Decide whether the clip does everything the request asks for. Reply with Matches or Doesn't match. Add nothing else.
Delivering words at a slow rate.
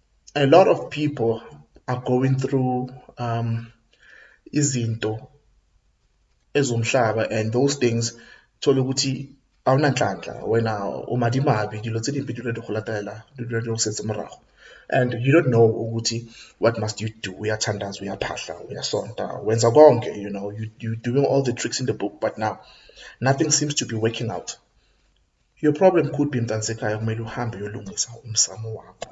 Doesn't match